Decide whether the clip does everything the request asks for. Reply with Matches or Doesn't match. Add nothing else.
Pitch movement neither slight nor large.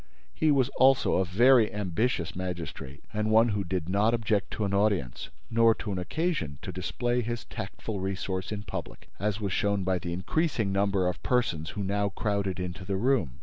Matches